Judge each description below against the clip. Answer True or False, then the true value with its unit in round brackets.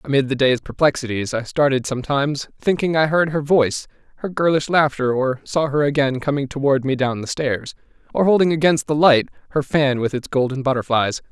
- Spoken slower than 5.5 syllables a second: False (5.6 syllables/s)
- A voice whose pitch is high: False (140 Hz)